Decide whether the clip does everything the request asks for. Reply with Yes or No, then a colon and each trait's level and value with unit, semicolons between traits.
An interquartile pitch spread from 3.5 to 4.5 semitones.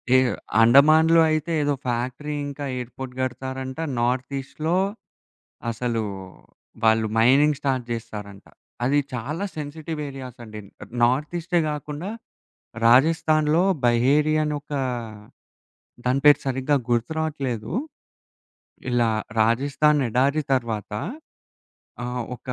Yes: average, 3.8 semitones